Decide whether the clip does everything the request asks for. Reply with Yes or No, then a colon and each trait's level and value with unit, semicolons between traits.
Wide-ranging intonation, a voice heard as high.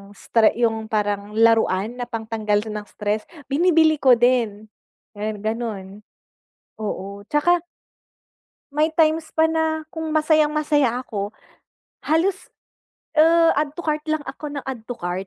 Yes: wide, 6.5 semitones; high, 240 Hz